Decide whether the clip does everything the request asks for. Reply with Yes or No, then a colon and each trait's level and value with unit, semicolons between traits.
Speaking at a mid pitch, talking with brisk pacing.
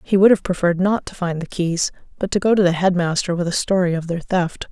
Yes: medium, 180 Hz; fast, 280 wpm